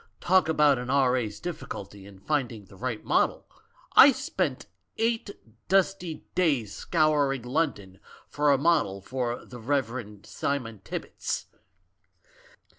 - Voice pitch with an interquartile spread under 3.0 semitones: No, wide, 5.6 semitones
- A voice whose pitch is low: Yes, low, 130 Hz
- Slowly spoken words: Yes, slow, 115 wpm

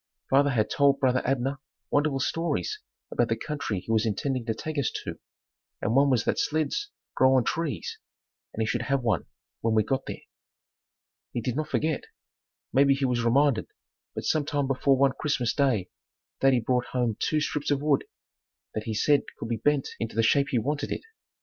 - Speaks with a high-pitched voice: No, low, 135 Hz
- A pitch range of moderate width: Yes, average, 3.7 semitones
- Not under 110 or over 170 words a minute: No, average, 190 wpm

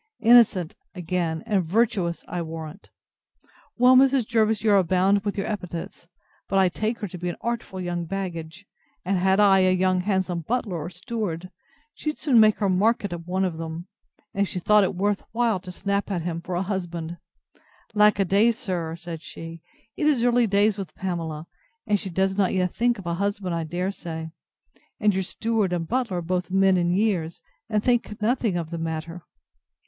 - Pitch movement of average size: Yes, average, 3.4 semitones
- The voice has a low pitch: No, high, 190 Hz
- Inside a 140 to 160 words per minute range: No, average, 190 wpm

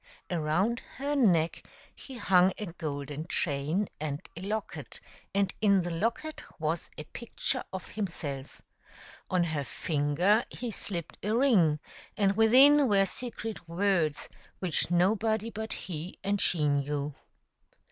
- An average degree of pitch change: No, wide, 5.7 semitones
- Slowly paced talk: Yes, slow, 130 wpm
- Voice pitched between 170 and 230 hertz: Yes, medium, 185 Hz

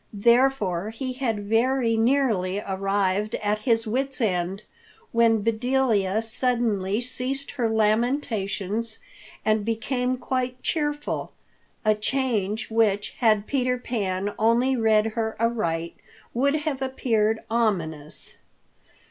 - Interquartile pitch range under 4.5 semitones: Yes, average, 3.5 semitones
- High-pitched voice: Yes, high, 225 Hz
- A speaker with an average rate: No, slow, 105 wpm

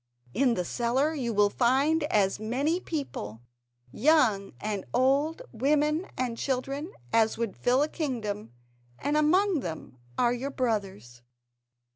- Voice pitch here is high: Yes, very high, 255 Hz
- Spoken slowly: Yes, slow, 130 wpm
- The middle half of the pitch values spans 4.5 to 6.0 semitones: Yes, wide, 5.6 semitones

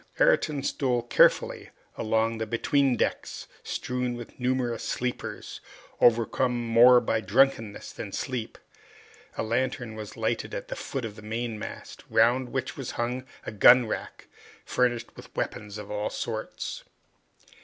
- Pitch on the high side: No, low, 120 Hz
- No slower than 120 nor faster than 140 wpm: Yes, slow, 135 wpm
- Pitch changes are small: Yes, narrow, 2.2 semitones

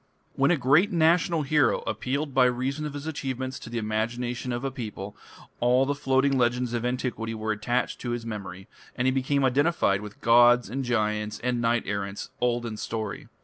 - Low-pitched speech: Yes, low, 125 Hz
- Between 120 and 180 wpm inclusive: No, average, 190 wpm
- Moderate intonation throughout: Yes, average, 3.1 semitones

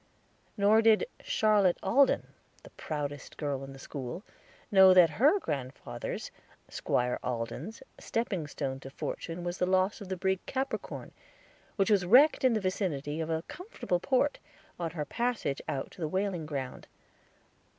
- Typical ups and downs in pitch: No, wide, 6.5 semitones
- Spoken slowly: No, average, 150 wpm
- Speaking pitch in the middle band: Yes, medium, 180 Hz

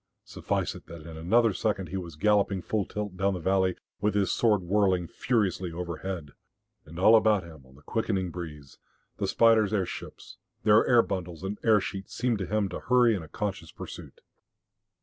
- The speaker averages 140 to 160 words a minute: No, average, 185 wpm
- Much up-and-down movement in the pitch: No, average, 3.4 semitones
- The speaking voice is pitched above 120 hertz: No, very low, 95 Hz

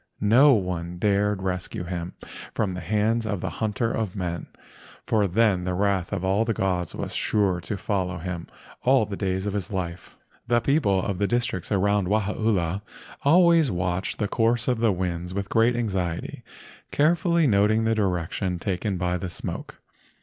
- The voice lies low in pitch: Yes, low, 100 Hz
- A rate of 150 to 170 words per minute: Yes, average, 165 wpm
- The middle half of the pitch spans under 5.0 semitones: Yes, average, 3.6 semitones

